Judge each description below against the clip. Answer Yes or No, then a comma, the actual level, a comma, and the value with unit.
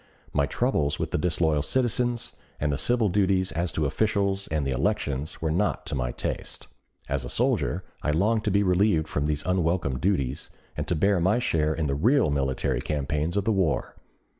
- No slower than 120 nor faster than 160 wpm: No, average, 190 wpm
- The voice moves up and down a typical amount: No, wide, 5.7 semitones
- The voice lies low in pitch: Yes, very low, 80 Hz